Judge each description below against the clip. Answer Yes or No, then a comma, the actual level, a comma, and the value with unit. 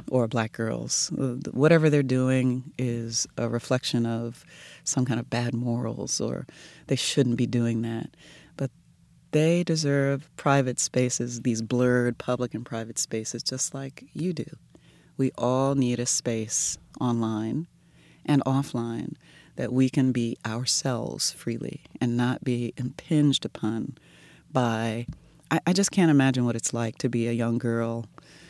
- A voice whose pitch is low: Yes, low, 125 Hz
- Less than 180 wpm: Yes, average, 145 wpm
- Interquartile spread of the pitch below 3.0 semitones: Yes, narrow, 2.6 semitones